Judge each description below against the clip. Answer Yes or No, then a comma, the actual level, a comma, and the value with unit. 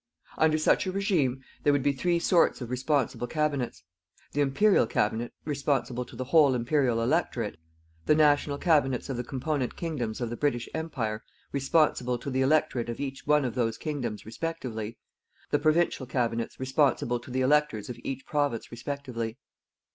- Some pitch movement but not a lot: Yes, average, 3.7 semitones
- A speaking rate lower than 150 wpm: No, average, 160 wpm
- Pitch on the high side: No, low, 135 Hz